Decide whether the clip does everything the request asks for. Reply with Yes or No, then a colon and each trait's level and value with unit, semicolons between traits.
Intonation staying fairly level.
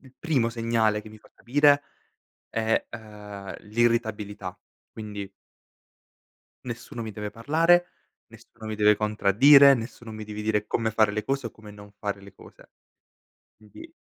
Yes: narrow, 2.1 semitones